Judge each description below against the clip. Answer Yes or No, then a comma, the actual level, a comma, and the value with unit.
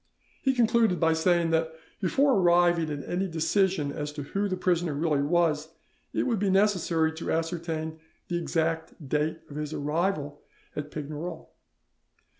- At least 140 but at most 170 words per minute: Yes, average, 150 wpm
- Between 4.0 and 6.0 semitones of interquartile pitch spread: No, average, 2.8 semitones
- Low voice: No, medium, 165 Hz